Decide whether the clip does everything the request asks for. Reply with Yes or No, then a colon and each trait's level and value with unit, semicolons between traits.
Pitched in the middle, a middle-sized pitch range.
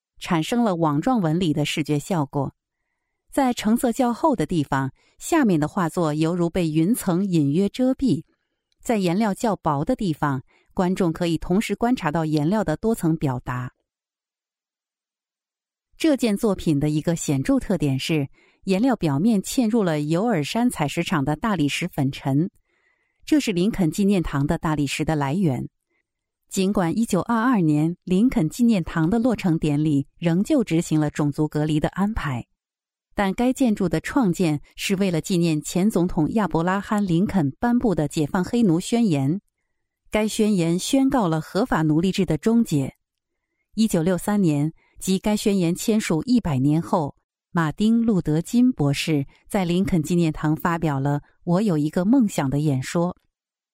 No: medium, 175 Hz; wide, 5.8 semitones